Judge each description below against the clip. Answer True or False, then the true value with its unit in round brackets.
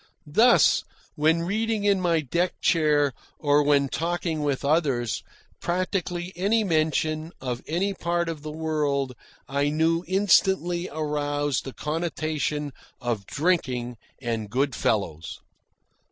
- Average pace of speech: False (120 wpm)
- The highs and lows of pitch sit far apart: False (3.6 semitones)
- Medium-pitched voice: True (155 Hz)